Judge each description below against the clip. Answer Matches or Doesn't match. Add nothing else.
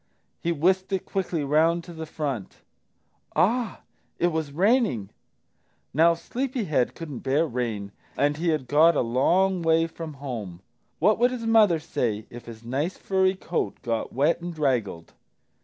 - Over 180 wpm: Doesn't match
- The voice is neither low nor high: Matches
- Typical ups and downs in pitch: Doesn't match